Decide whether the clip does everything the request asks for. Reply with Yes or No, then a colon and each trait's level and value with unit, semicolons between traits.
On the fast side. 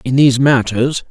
No: average, 165 wpm